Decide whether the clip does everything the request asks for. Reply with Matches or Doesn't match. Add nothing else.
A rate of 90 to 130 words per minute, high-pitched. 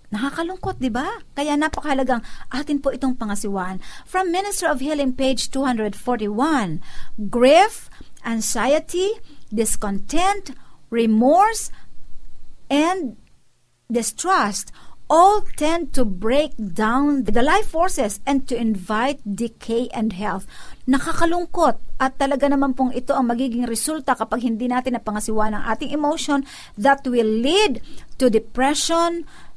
Matches